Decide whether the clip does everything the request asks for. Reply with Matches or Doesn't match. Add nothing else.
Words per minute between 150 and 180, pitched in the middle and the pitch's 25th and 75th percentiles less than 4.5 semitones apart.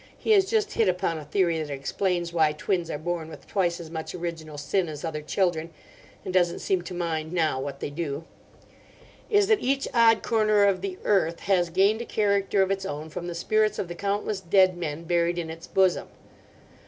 Doesn't match